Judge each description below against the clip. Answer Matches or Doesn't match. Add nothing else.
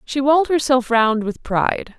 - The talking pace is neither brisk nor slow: Matches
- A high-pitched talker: Matches